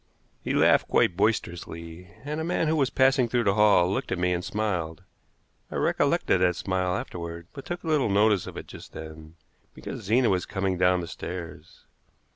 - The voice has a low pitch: Yes, very low, 95 Hz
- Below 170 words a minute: No, average, 185 wpm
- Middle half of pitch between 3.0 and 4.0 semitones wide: No, average, 4.7 semitones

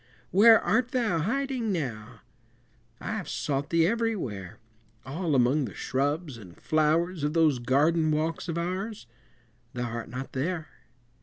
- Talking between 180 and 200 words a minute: No, average, 140 wpm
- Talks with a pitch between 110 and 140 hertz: No, medium, 155 Hz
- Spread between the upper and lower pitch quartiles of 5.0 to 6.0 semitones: Yes, wide, 5.6 semitones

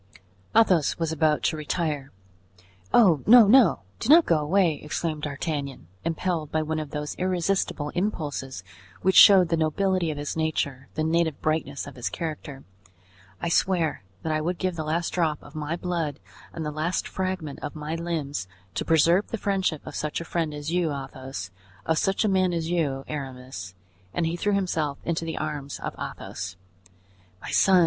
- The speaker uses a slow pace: No, average, 175 wpm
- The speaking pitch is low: No, medium, 160 Hz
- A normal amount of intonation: Yes, average, 3.1 semitones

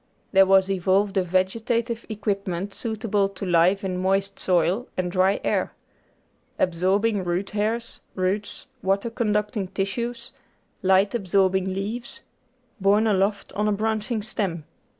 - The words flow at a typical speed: No, slow, 125 wpm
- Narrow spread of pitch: Yes, narrow, 2.3 semitones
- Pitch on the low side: No, high, 195 Hz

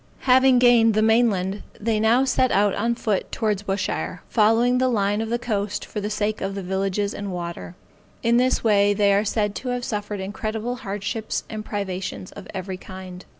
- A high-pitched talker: Yes, high, 210 Hz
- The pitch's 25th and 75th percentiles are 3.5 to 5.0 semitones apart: No, average, 2.7 semitones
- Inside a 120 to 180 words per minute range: No, average, 190 wpm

